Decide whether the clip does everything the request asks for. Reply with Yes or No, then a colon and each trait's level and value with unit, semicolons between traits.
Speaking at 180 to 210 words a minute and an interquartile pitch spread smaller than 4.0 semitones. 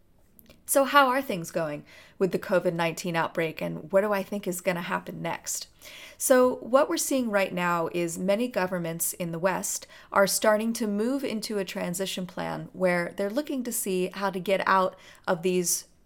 Yes: average, 190 wpm; average, 3.4 semitones